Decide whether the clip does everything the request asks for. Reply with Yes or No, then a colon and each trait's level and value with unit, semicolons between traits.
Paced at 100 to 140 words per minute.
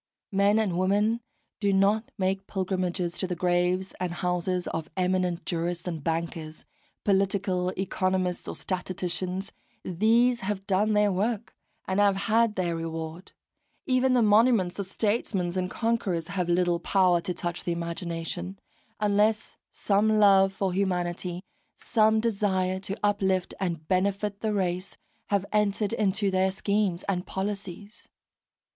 Yes: slow, 135 wpm